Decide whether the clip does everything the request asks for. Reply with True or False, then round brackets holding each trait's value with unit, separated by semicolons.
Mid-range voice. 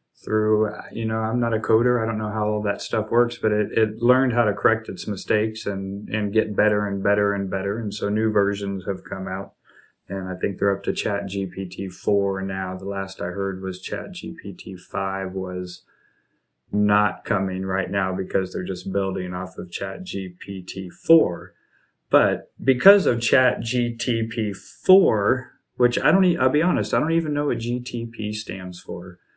False (105 Hz)